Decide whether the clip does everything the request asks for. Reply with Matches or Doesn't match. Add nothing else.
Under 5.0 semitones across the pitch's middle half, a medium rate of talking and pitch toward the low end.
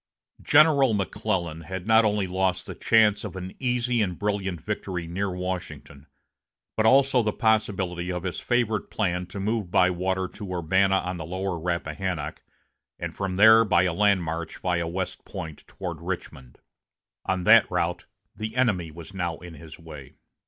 Matches